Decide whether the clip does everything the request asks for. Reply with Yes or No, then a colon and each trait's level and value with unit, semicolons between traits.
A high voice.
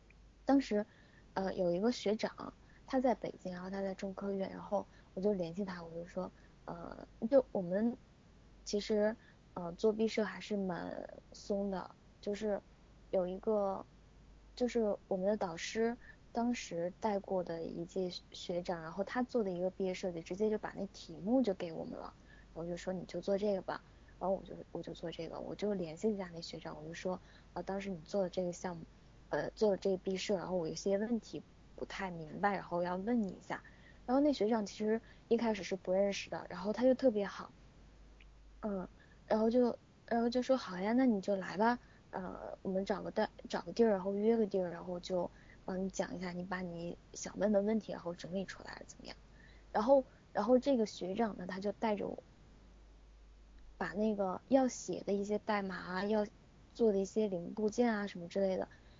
Yes: high, 195 Hz